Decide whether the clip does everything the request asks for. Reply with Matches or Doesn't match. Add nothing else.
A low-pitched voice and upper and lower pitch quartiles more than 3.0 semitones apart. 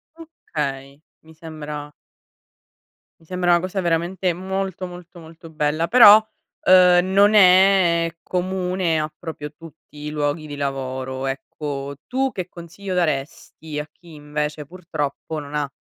Doesn't match